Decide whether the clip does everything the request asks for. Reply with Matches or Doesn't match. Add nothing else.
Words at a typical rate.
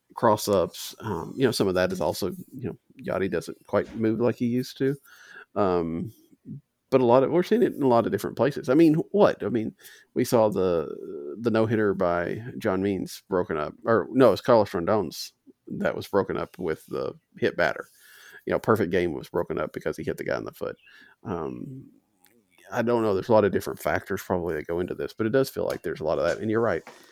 Doesn't match